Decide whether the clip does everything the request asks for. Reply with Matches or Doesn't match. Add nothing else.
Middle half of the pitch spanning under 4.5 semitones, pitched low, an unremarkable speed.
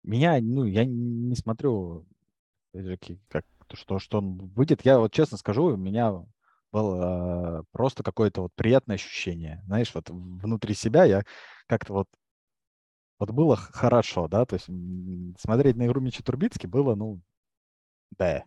Doesn't match